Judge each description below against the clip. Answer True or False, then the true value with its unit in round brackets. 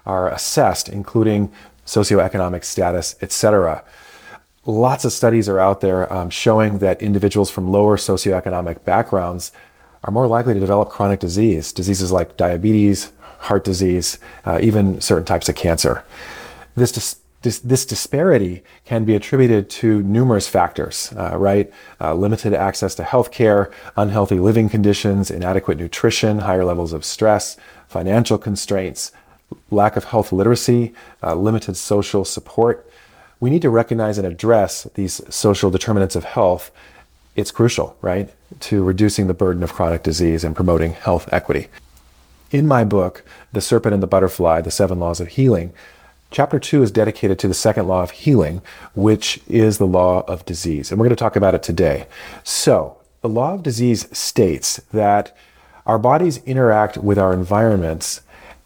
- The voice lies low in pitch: True (100 Hz)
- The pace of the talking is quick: False (155 wpm)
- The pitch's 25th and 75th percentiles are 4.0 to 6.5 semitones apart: False (3.3 semitones)